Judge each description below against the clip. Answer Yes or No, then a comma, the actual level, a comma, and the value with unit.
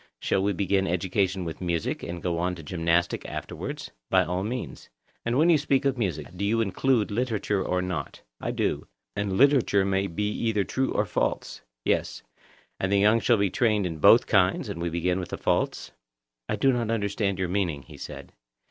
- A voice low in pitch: Yes, low, 100 Hz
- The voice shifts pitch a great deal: No, average, 3.9 semitones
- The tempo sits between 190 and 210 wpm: Yes, average, 195 wpm